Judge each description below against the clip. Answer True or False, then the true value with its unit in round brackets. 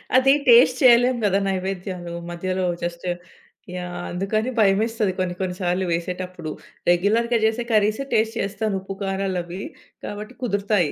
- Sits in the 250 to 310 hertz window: False (195 Hz)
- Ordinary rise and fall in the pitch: True (3.4 semitones)